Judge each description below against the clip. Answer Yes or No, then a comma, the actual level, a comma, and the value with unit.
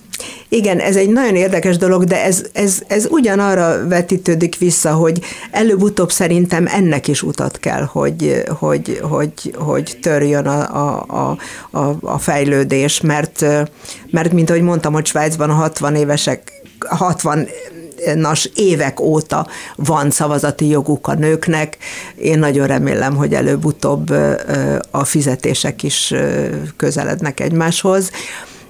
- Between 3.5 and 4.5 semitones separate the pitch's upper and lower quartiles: Yes, average, 3.9 semitones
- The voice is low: No, medium, 160 Hz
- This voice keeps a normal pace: Yes, average, 125 wpm